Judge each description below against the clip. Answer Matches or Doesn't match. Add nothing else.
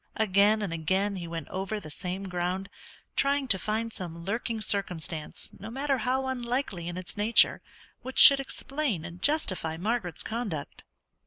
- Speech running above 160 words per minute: Doesn't match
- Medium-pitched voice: Doesn't match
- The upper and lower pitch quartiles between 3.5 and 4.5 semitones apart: Doesn't match